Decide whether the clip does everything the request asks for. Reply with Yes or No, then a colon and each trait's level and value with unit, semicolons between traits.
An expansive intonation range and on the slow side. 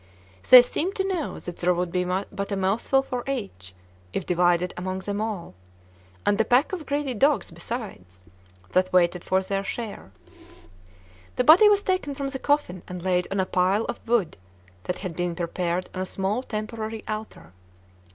No: wide, 5.7 semitones; average, 175 wpm